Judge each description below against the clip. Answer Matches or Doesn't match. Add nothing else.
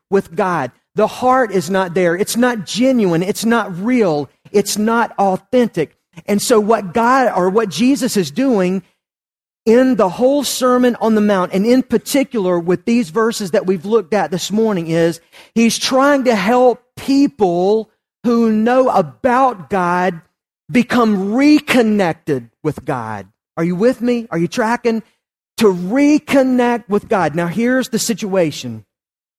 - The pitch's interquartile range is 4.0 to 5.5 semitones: Matches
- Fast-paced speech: Doesn't match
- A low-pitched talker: Doesn't match